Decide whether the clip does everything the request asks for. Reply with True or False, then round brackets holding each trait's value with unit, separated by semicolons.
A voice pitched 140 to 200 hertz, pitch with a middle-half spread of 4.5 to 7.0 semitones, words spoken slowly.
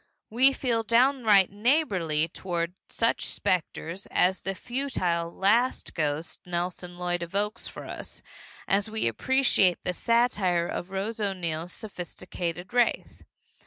True (190 Hz; 4.8 semitones; 120 wpm)